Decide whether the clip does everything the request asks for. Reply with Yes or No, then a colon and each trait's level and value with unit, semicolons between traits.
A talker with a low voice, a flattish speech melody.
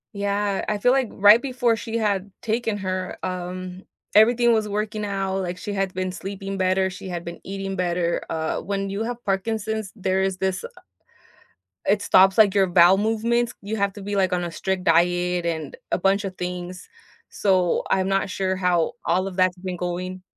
No: high, 190 Hz; narrow, 2.0 semitones